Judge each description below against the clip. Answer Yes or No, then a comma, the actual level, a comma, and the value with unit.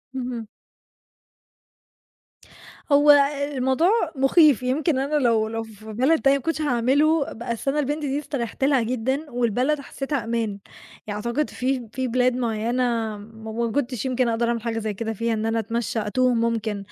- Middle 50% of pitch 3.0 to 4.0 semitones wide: Yes, average, 3.3 semitones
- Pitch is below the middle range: No, high, 245 Hz